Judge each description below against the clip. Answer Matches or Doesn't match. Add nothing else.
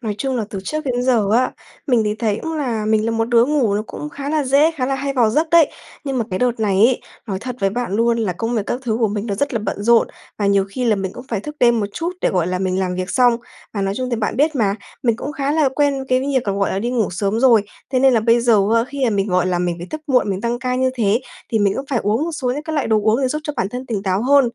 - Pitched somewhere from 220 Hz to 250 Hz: Matches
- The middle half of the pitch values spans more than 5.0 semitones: Doesn't match